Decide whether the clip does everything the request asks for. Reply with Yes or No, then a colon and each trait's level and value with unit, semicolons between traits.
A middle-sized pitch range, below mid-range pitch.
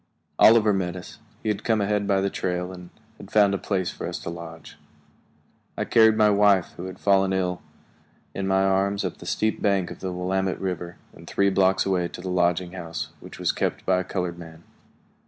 No: narrow, 1.8 semitones; very low, 95 Hz